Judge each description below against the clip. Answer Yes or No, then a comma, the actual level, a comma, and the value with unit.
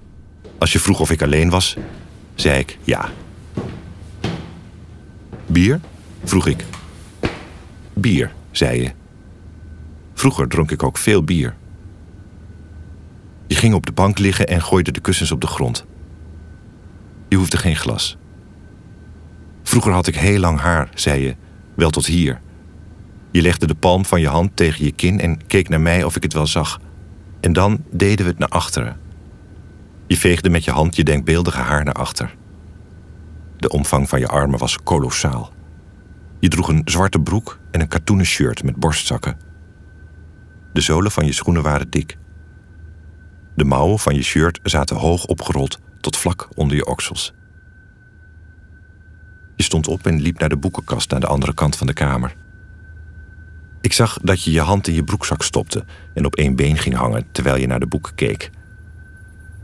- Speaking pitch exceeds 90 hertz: No, very low, 85 Hz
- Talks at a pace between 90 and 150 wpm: No, average, 160 wpm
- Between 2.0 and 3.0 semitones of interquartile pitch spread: Yes, average, 2.7 semitones